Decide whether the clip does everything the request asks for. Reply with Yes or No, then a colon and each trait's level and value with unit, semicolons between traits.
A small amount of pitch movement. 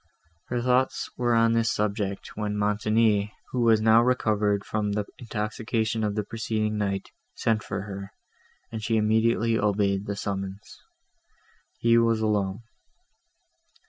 Yes: narrow, 1.9 semitones